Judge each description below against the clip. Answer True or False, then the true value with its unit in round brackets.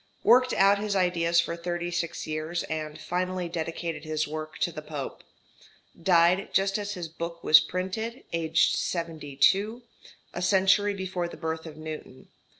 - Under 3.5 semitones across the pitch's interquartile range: True (3.0 semitones)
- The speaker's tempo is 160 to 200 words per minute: False (150 wpm)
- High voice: False (170 Hz)